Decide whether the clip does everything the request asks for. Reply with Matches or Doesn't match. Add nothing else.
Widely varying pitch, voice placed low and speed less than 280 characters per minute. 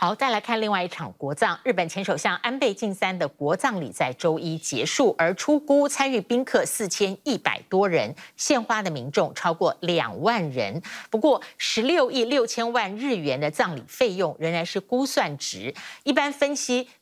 Doesn't match